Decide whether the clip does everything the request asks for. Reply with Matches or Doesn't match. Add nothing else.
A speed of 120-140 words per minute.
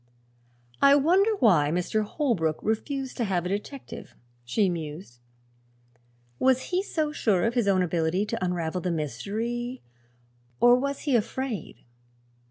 Matches